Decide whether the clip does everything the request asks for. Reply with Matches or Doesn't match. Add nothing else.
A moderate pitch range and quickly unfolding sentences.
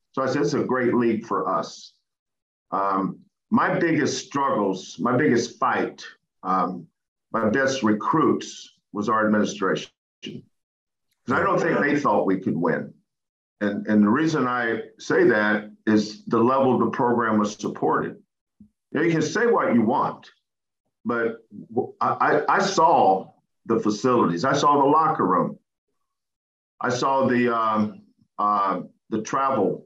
Doesn't match